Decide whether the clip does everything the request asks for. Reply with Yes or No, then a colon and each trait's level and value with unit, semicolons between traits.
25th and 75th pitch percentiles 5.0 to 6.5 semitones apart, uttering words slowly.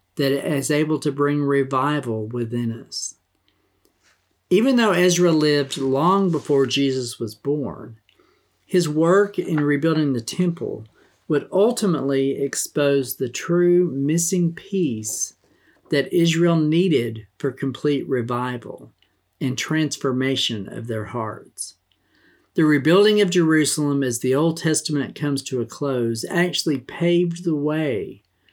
No: average, 4.5 semitones; slow, 120 wpm